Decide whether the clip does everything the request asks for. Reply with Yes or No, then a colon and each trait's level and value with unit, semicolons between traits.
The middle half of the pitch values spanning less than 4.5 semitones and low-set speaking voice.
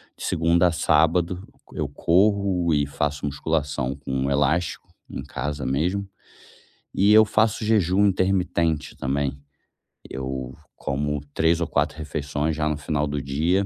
Yes: average, 4.1 semitones; very low, 80 Hz